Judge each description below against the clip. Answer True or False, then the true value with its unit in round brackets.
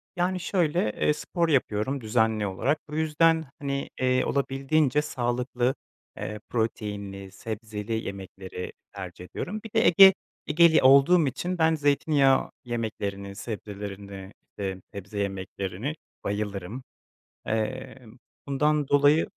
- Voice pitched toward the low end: True (125 Hz)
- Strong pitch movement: True (6.7 semitones)